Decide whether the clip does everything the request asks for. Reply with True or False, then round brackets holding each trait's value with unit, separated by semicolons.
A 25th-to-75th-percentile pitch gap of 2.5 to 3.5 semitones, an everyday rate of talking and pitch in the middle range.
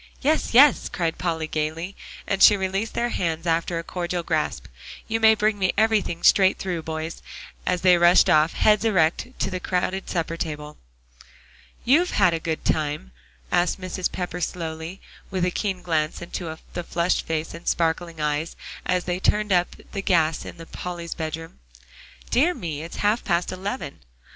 True (2.9 semitones; 170 wpm; 175 Hz)